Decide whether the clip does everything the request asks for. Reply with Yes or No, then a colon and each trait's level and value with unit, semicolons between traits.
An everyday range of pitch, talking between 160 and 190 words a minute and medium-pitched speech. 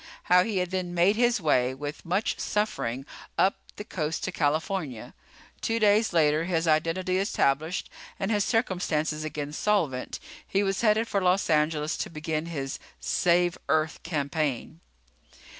No: average, 4.1 semitones; average, 145 wpm; medium, 170 Hz